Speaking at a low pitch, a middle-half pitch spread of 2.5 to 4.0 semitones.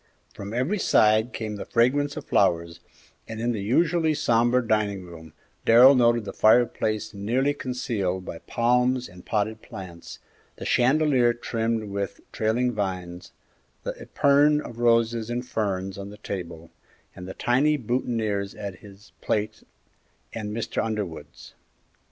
Yes: low, 110 Hz; average, 3.7 semitones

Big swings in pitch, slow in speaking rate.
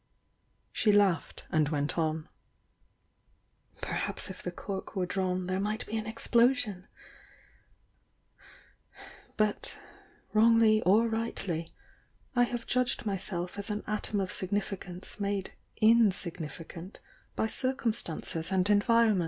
No: average, 3.4 semitones; slow, 110 wpm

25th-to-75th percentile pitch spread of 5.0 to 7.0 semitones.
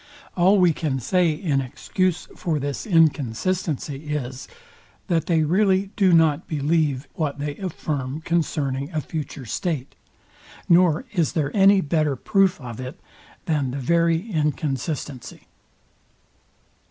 No: average, 3.9 semitones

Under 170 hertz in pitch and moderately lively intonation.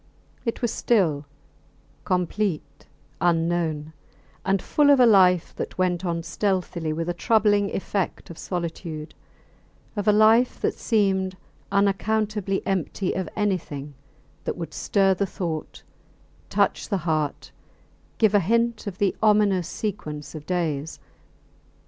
No: high, 190 Hz; average, 3.8 semitones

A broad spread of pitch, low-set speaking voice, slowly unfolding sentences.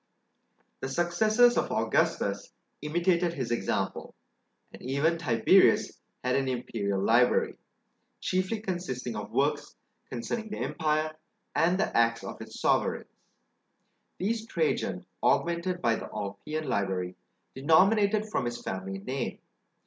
No: wide, 7.6 semitones; medium, 150 Hz; slow, 120 wpm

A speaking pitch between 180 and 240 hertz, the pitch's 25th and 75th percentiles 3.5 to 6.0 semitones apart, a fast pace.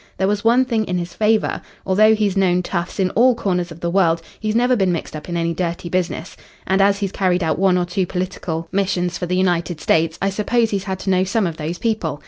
No: medium, 185 Hz; average, 2.8 semitones; fast, 245 wpm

